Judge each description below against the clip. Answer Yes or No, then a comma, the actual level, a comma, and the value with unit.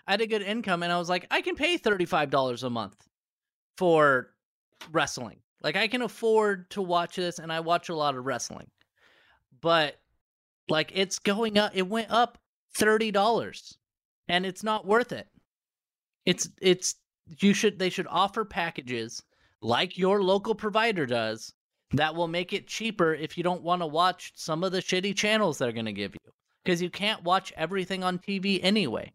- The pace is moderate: Yes, average, 180 wpm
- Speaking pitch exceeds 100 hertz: Yes, medium, 185 Hz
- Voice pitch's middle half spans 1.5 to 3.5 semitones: No, average, 4.4 semitones